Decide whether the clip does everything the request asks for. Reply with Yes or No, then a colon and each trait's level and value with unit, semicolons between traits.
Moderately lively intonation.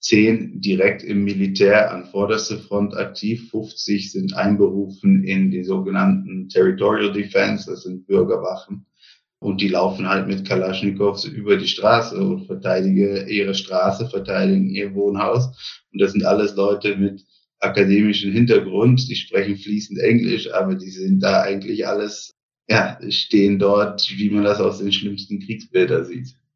Yes: average, 4.1 semitones